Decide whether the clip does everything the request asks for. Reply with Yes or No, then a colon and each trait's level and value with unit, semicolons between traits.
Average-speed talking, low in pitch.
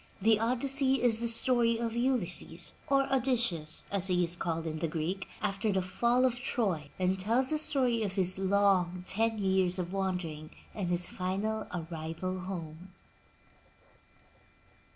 No: average, 150 wpm; high, 195 Hz